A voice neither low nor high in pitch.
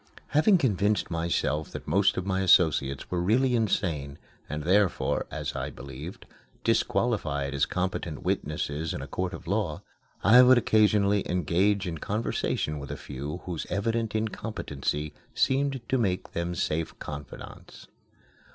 No: very low, 90 Hz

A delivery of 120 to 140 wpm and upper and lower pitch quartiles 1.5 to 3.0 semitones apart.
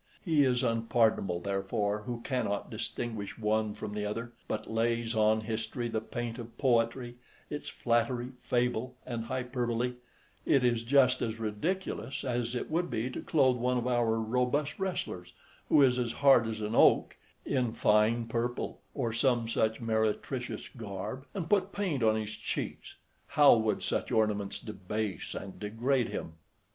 No: average, 155 wpm; narrow, 2.5 semitones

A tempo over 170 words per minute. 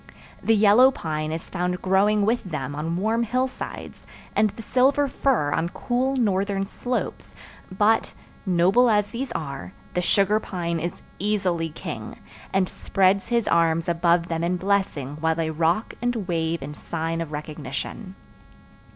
No: average, 150 wpm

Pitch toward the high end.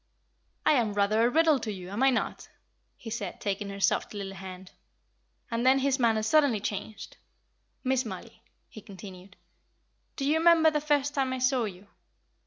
Yes: high, 230 Hz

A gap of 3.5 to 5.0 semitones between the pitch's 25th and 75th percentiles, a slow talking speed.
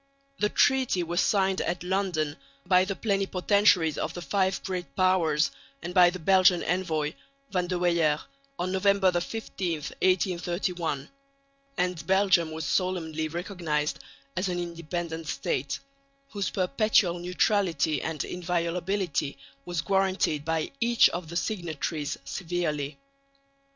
No: average, 2.7 semitones; slow, 120 wpm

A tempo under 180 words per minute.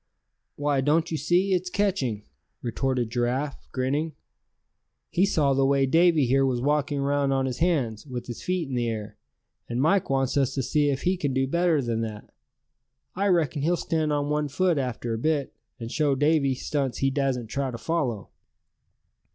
No: average, 185 wpm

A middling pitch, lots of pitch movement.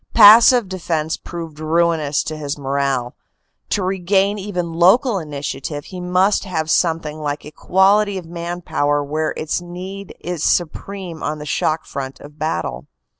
No: medium, 165 Hz; average, 3.8 semitones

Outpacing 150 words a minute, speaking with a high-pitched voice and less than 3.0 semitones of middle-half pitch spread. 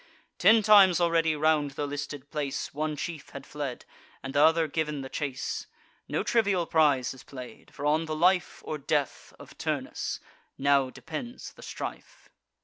No: average, 160 wpm; medium, 150 Hz; narrow, 2.6 semitones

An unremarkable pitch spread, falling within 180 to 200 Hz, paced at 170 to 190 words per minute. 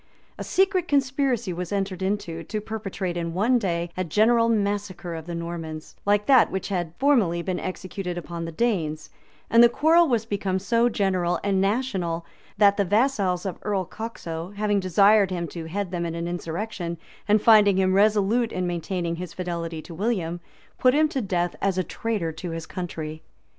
Yes: average, 4.0 semitones; high, 190 Hz; average, 180 wpm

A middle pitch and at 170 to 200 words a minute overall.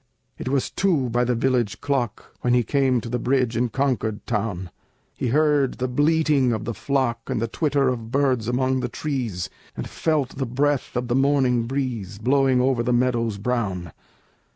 No: low, 125 Hz; average, 180 wpm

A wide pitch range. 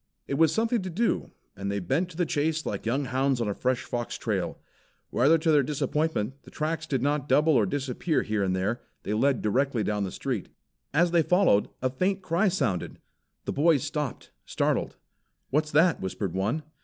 Yes: wide, 5.8 semitones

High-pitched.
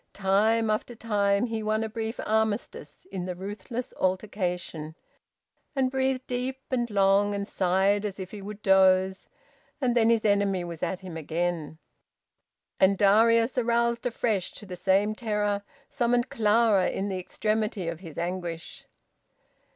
Yes: high, 205 Hz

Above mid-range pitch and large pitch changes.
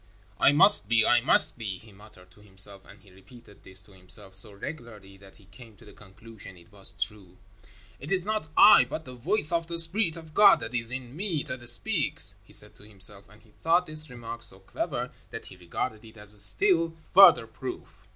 No: low, 115 Hz; wide, 6.8 semitones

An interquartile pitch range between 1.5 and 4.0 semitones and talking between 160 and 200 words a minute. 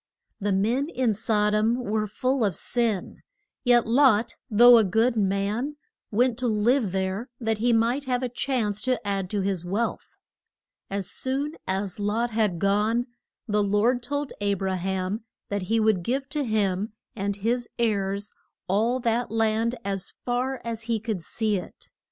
Yes: average, 3.3 semitones; average, 165 wpm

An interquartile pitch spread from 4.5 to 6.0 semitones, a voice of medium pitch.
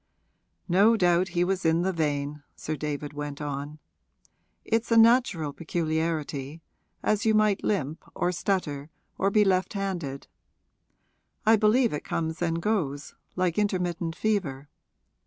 Yes: average, 5.0 semitones; medium, 170 Hz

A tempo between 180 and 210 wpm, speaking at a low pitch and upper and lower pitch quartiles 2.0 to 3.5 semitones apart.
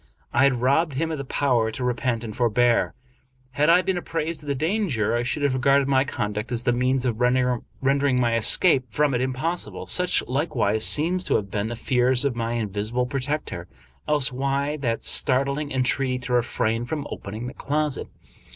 Yes: average, 190 wpm; low, 130 Hz; average, 3.2 semitones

